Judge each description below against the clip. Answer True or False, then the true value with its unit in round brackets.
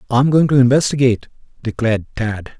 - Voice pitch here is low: True (125 Hz)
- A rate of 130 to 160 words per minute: True (140 wpm)